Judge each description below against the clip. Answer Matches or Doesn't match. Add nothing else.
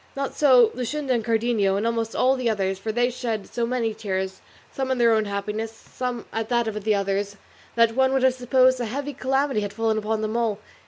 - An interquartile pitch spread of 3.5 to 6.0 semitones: Doesn't match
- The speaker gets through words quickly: Matches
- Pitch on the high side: Matches